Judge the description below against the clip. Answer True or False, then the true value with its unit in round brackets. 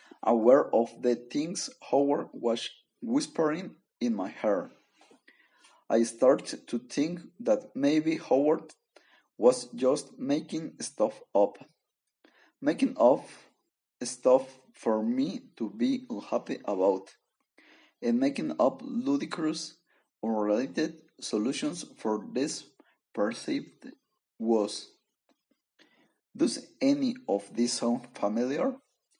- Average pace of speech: False (95 wpm)